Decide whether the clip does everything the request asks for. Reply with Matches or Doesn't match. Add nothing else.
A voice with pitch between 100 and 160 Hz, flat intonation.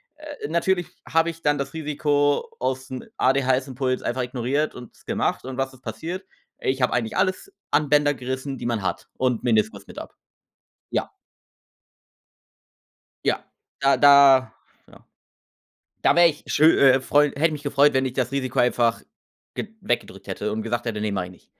Doesn't match